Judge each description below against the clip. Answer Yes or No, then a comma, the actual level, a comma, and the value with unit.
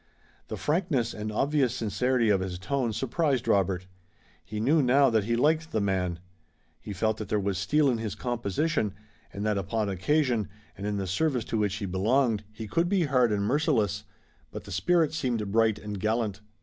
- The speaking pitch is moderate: No, low, 110 Hz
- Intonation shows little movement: No, average, 5.1 semitones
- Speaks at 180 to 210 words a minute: Yes, average, 190 wpm